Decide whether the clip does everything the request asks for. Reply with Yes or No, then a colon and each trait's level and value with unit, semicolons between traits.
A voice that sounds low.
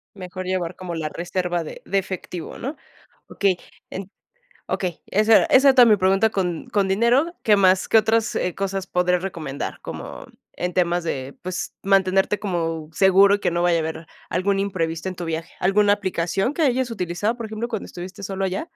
No: high, 190 Hz